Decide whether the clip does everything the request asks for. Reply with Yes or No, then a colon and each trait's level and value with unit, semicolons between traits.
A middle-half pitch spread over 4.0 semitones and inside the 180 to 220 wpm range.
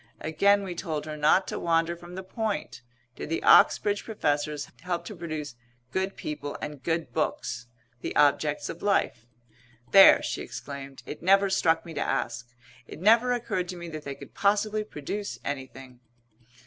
No: average, 4.9 semitones; average, 165 wpm